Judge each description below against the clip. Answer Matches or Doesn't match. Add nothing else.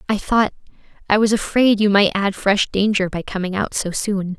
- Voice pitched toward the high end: Matches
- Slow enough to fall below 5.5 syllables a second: Matches